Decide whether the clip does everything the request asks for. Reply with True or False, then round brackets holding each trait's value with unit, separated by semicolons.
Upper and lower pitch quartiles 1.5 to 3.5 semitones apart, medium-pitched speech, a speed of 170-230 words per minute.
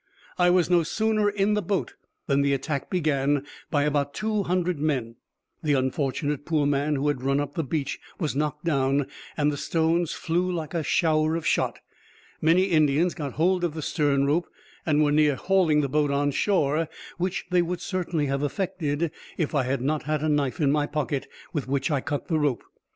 True (3.2 semitones; 150 Hz; 200 wpm)